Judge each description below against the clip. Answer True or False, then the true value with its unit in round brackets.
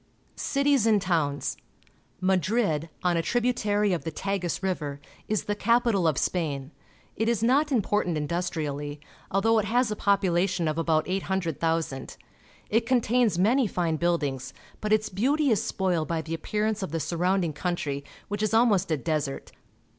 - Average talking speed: True (160 wpm)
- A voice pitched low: False (185 Hz)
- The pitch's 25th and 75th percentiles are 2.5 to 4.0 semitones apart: False (4.9 semitones)